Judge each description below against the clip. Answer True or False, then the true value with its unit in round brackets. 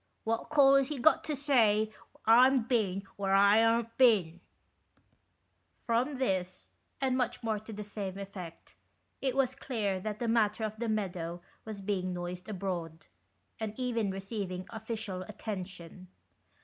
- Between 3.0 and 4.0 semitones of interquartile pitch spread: True (3.7 semitones)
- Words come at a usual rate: True (150 wpm)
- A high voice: True (215 Hz)